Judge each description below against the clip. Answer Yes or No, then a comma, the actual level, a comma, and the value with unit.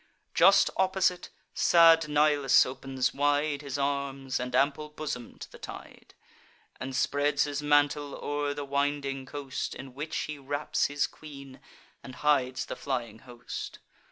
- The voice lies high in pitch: No, medium, 145 Hz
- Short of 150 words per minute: Yes, average, 140 wpm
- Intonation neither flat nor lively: No, narrow, 1.7 semitones